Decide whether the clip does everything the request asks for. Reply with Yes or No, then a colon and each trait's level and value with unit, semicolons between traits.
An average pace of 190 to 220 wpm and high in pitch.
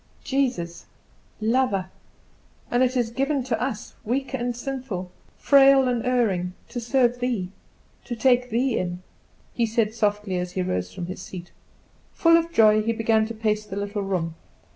No: average, 165 wpm; high, 225 Hz